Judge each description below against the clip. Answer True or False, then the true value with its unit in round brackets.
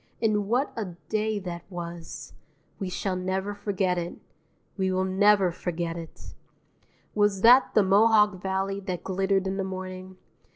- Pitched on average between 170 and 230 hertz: True (190 Hz)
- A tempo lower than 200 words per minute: True (150 wpm)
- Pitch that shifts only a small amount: True (2.0 semitones)